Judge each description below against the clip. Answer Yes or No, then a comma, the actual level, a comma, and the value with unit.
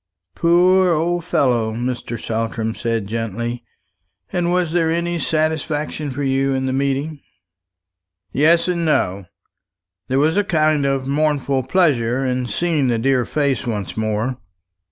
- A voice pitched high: No, medium, 140 Hz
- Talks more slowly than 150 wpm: Yes, slow, 135 wpm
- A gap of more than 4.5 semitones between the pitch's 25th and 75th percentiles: Yes, average, 5.1 semitones